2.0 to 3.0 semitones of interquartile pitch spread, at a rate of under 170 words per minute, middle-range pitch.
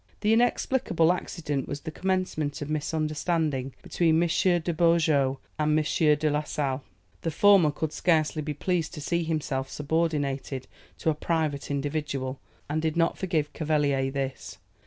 Yes: narrow, 2.6 semitones; average, 150 wpm; medium, 155 Hz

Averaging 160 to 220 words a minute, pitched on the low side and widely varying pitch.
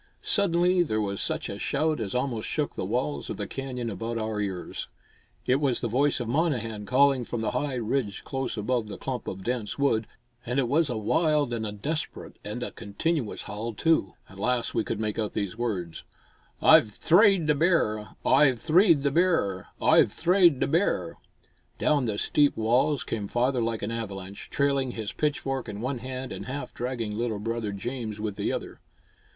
No: average, 190 wpm; low, 120 Hz; average, 4.7 semitones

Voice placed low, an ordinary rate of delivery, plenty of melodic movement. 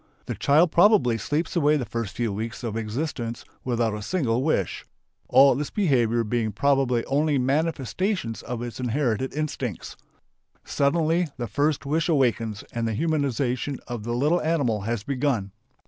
No: low, 130 Hz; average, 155 wpm; average, 4.5 semitones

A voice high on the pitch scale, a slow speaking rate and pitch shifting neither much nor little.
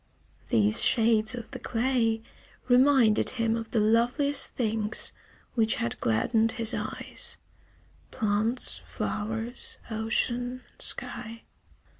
No: high, 225 Hz; slow, 100 wpm; narrow, 2.0 semitones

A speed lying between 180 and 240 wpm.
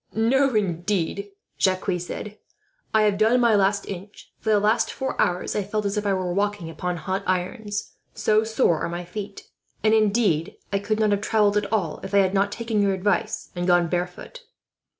Yes: average, 190 wpm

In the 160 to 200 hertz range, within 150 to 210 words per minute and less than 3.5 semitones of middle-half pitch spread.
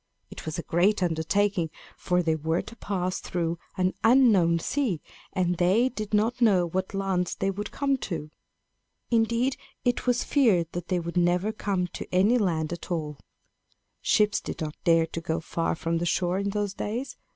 No: medium, 185 Hz; average, 180 wpm; average, 4.0 semitones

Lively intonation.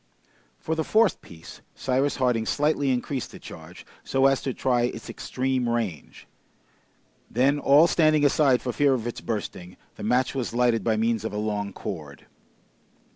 No: average, 3.7 semitones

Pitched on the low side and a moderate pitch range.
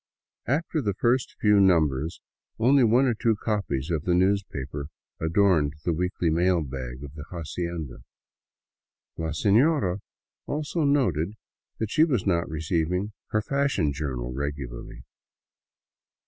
No: very low, 90 Hz; wide, 6.5 semitones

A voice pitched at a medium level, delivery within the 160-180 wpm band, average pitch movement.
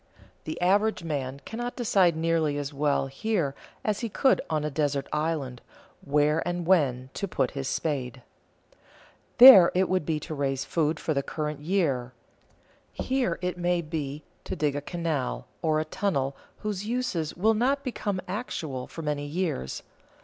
Yes: medium, 160 Hz; average, 165 wpm; average, 4.7 semitones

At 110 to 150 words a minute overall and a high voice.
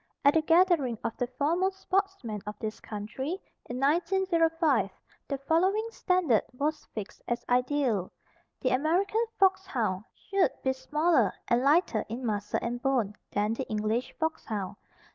Yes: average, 140 wpm; very high, 270 Hz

